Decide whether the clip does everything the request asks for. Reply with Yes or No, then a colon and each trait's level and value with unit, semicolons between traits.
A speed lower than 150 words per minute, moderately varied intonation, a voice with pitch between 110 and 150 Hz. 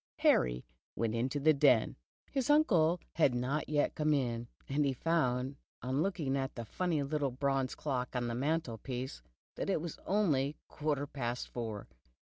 No: average, 160 wpm; average, 3.8 semitones; medium, 140 Hz